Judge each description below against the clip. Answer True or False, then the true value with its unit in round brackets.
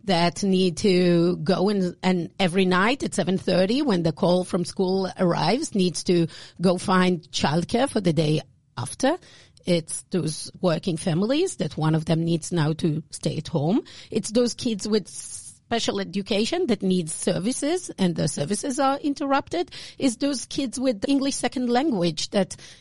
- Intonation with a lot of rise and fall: True (5.8 semitones)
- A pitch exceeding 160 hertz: True (185 Hz)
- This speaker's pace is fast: False (160 wpm)